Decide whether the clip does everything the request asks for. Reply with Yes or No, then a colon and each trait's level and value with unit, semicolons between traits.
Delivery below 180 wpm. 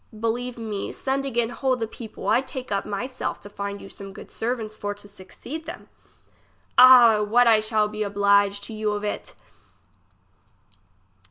Yes: average, 170 wpm